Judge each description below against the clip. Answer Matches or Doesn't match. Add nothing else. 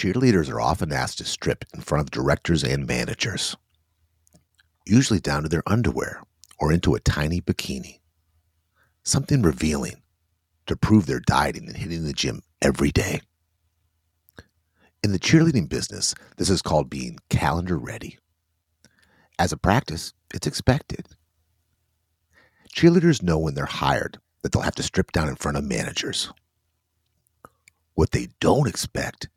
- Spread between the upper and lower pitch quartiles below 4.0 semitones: Matches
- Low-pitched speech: Matches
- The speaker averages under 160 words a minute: Matches